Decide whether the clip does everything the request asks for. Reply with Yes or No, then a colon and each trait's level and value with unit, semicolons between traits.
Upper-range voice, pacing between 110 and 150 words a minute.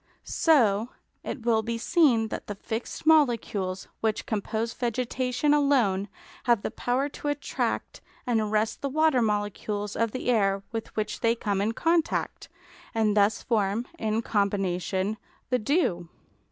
Yes: high, 225 Hz; average, 140 wpm